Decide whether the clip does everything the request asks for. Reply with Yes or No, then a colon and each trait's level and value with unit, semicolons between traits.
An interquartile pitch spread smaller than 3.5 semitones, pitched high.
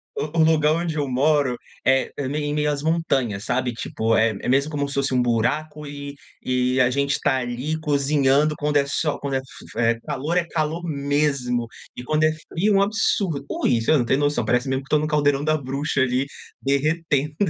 No: average, 2.8 semitones; medium, 140 Hz